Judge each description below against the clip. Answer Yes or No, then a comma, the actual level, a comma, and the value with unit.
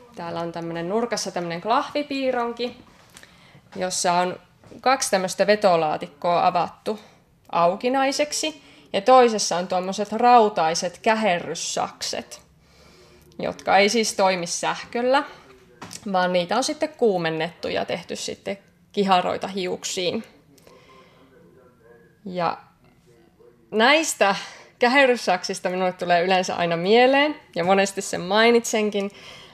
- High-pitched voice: Yes, high, 200 Hz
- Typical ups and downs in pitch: Yes, average, 5.0 semitones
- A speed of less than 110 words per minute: Yes, slow, 95 wpm